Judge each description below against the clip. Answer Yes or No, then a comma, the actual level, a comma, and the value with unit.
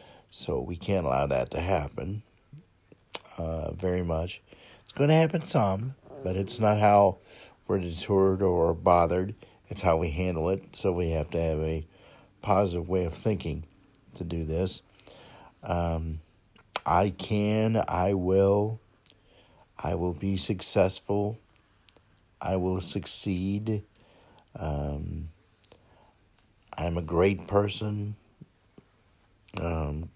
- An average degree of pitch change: Yes, average, 3.4 semitones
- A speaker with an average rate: No, slow, 115 wpm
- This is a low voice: Yes, very low, 95 Hz